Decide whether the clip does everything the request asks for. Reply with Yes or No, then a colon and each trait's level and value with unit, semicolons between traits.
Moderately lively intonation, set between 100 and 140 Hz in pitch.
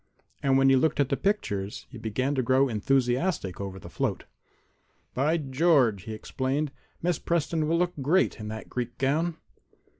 Yes: average, 5.0 semitones; low, 135 Hz